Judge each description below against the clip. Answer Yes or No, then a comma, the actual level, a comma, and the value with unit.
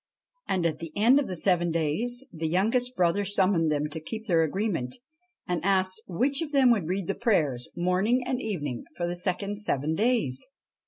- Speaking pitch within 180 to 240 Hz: Yes, medium, 185 Hz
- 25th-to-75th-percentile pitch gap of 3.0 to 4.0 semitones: No, average, 5.2 semitones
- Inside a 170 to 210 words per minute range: Yes, average, 190 wpm